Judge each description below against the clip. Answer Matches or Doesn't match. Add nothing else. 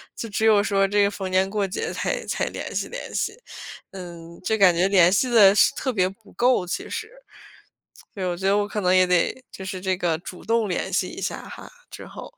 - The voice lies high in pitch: Matches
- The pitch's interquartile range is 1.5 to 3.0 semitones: Matches